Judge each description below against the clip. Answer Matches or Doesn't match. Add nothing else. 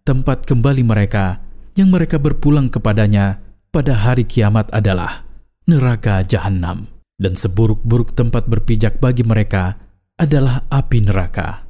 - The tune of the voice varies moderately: Matches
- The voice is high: Doesn't match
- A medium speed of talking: Matches